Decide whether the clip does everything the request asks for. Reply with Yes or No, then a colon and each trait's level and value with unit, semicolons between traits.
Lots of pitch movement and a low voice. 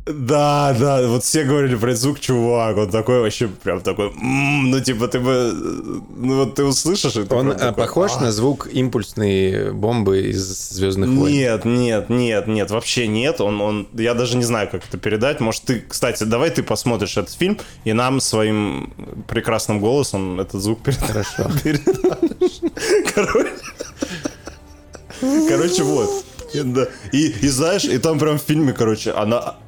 No: average, 4.6 semitones; low, 125 Hz